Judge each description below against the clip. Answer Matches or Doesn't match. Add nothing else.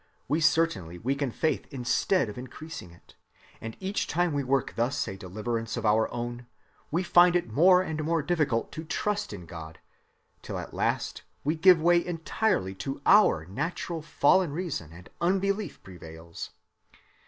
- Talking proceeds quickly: Doesn't match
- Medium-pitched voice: Matches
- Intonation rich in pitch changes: Matches